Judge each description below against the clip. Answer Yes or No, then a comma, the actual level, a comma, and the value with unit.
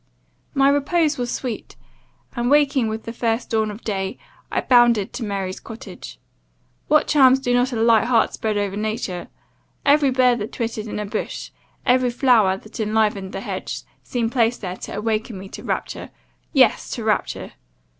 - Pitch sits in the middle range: No, high, 230 Hz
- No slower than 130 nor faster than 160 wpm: No, average, 170 wpm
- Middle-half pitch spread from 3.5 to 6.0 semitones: No, average, 3.1 semitones